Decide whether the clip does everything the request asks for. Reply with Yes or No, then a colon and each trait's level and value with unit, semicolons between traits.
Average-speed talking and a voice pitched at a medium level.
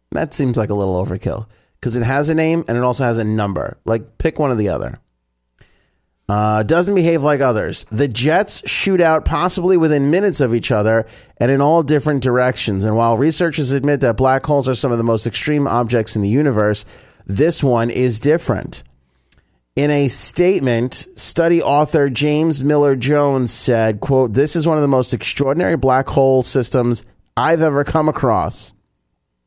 No: average, 180 wpm; low, 130 Hz